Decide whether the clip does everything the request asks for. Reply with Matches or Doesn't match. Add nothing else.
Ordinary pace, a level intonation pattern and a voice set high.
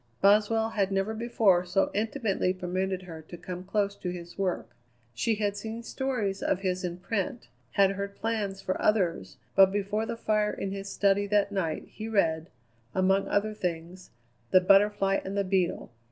Matches